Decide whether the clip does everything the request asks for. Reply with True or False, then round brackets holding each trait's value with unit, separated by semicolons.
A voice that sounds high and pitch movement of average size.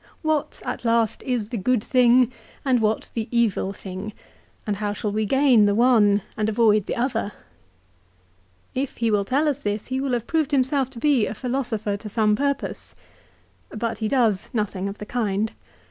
True (230 Hz; 3.5 semitones)